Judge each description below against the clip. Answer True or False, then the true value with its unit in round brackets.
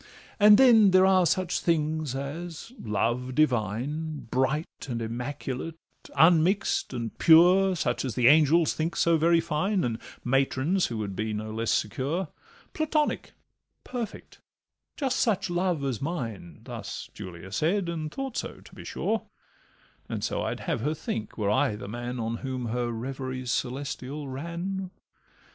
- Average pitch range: False (6.2 semitones)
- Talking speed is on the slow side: False (145 wpm)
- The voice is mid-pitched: True (145 Hz)